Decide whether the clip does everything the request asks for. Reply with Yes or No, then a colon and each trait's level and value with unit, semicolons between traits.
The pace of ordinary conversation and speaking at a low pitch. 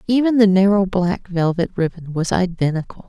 No: average, 155 wpm; medium, 185 Hz